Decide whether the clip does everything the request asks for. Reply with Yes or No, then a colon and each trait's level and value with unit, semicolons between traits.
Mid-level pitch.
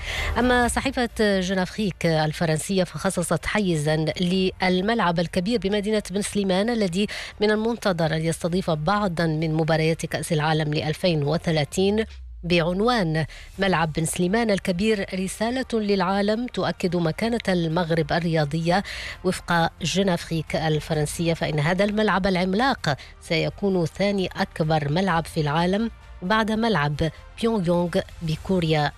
Yes: medium, 180 Hz